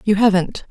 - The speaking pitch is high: Yes, high, 200 Hz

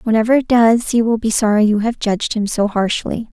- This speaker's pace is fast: Yes, fast, 230 wpm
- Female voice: Yes, female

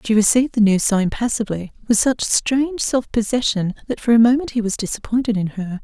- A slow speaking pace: No, fast, 205 wpm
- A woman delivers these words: Yes, female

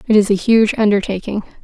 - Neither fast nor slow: Yes, average, 185 wpm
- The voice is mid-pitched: No, high, 210 Hz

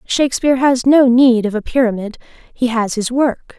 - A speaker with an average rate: Yes, average, 185 wpm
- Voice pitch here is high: Yes, high, 245 Hz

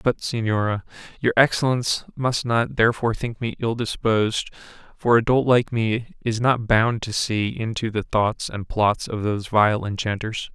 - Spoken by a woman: No, male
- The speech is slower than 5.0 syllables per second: Yes, 4.7 syllables/s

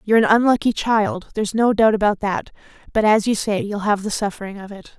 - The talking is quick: Yes, fast, 230 wpm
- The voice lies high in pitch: Yes, high, 210 Hz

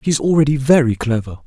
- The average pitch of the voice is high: No, low, 135 Hz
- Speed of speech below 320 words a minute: Yes, fast, 205 wpm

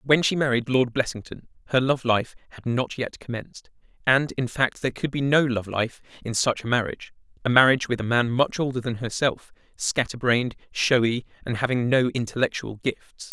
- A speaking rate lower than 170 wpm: No, average, 185 wpm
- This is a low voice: Yes, low, 125 Hz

